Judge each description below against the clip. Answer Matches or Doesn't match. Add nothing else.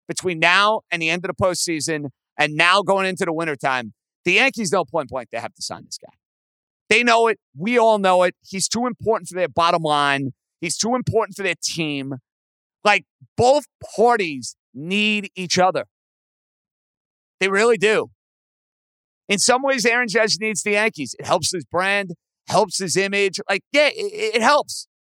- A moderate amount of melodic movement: Matches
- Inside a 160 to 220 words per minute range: Matches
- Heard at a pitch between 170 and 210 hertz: Matches